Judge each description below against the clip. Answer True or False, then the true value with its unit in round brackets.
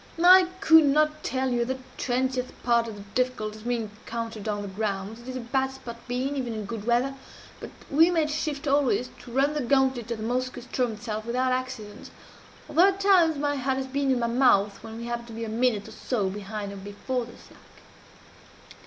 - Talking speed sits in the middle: False (215 wpm)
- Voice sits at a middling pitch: False (245 Hz)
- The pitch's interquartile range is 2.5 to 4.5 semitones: True (3.2 semitones)